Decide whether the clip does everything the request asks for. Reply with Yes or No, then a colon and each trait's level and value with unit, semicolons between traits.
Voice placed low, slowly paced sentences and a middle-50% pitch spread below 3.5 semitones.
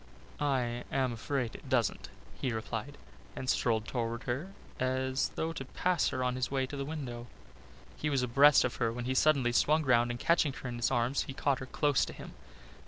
No: low, 130 Hz; fast, 205 wpm; narrow, 2.6 semitones